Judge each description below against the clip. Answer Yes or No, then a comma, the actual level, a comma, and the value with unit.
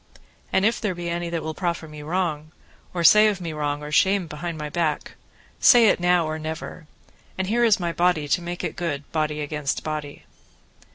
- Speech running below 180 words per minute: No, fast, 205 wpm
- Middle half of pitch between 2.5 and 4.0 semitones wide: Yes, average, 2.9 semitones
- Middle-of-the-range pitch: Yes, medium, 170 Hz